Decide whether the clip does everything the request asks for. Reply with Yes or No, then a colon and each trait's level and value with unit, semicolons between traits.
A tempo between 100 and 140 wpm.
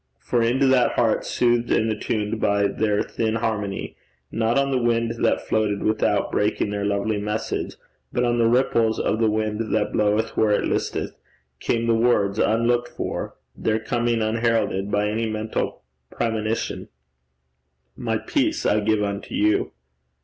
No: average, 155 wpm